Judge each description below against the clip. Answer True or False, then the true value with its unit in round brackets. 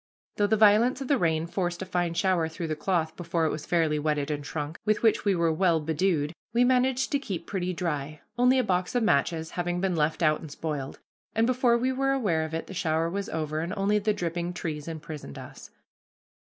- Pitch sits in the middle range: True (175 Hz)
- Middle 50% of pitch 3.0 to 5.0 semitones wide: True (4.6 semitones)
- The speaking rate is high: True (220 wpm)